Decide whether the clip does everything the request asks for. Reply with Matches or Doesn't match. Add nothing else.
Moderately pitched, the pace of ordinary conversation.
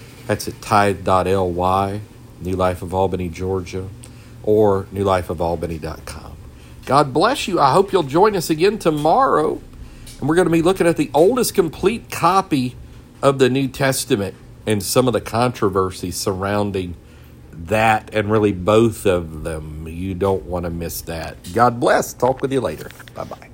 Doesn't match